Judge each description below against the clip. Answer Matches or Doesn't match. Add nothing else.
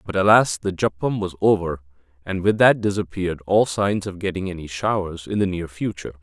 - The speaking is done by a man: Matches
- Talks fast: Doesn't match